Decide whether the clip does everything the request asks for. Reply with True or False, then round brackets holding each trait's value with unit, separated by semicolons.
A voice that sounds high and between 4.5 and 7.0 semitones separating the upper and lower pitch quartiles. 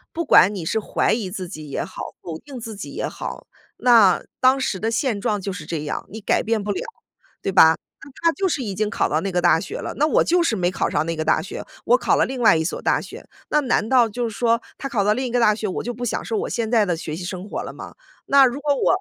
True (215 Hz; 5.2 semitones)